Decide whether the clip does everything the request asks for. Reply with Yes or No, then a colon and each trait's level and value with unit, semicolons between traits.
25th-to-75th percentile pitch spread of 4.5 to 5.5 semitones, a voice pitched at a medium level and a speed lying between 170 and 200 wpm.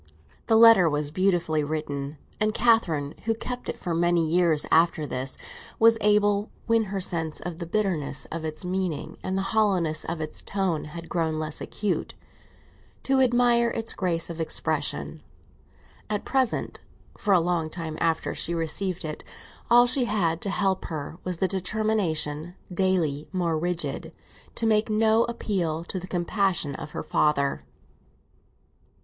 No: average, 4.9 semitones; medium, 175 Hz; average, 155 wpm